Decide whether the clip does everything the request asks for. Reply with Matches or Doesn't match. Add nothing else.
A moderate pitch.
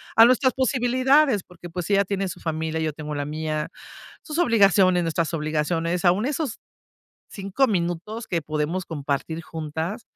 Matches